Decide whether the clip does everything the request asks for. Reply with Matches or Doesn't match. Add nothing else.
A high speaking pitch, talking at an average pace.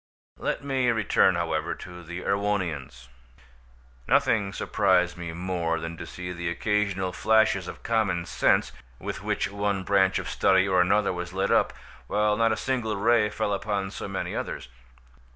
Doesn't match